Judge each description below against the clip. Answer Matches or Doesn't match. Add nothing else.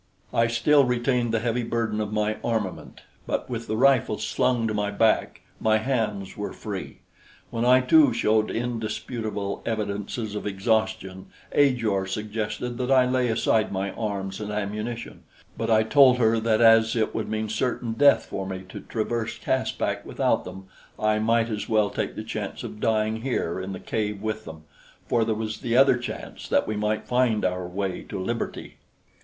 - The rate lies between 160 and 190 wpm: Matches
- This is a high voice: Doesn't match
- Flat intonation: Matches